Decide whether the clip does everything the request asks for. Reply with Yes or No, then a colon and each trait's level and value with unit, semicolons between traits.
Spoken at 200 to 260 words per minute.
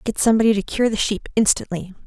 Yes: fast, 205 wpm